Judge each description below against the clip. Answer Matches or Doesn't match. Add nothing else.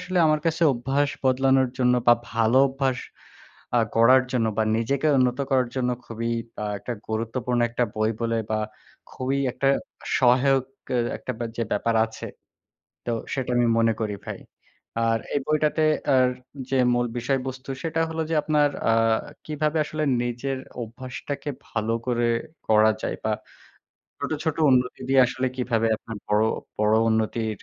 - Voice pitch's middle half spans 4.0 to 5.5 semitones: Doesn't match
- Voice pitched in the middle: Doesn't match